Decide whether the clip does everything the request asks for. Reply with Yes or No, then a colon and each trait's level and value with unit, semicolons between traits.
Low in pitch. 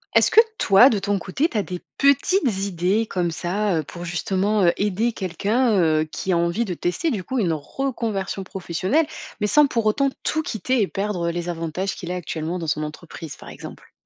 No: high, 195 Hz